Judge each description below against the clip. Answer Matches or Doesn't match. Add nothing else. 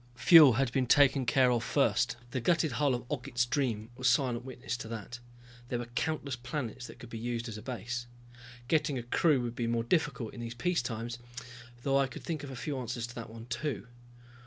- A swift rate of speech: Matches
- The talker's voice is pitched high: Doesn't match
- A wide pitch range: Doesn't match